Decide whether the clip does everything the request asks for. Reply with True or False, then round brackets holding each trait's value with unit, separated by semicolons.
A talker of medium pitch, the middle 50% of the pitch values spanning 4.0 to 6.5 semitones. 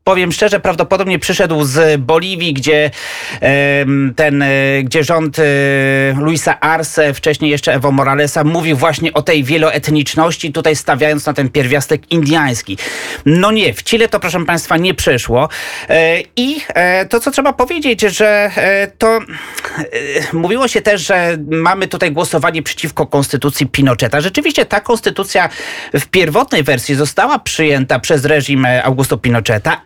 True (160 Hz; 4.4 semitones)